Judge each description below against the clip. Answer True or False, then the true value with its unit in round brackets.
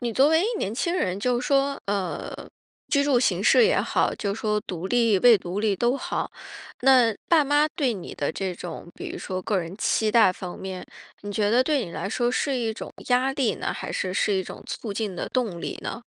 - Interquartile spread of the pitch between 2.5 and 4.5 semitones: False (5.2 semitones)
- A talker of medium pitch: False (225 Hz)